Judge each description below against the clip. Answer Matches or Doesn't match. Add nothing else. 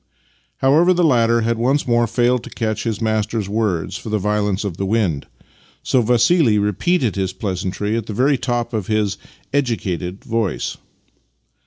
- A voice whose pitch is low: Matches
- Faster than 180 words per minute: Doesn't match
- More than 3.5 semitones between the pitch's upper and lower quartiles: Doesn't match